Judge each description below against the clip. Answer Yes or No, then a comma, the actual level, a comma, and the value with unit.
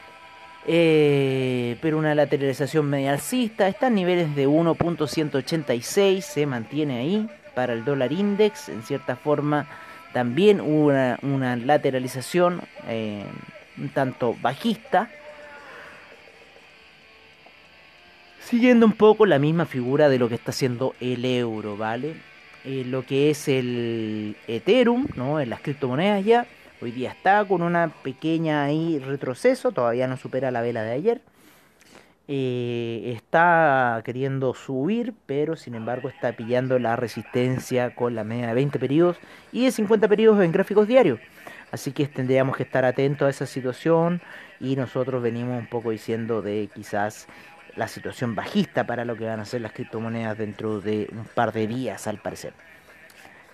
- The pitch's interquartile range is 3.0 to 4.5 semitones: No, wide, 5.4 semitones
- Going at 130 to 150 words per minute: Yes, average, 145 wpm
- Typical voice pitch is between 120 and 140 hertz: Yes, low, 135 Hz